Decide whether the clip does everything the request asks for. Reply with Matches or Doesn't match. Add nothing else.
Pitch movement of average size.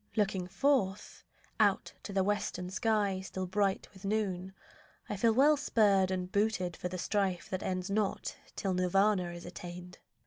Doesn't match